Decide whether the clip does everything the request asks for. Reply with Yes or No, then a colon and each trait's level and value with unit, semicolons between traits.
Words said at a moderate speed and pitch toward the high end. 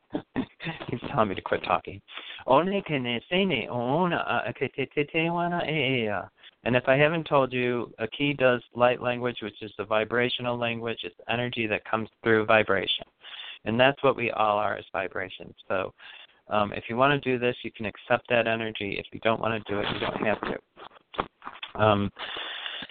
No: average, 160 wpm; low, 120 Hz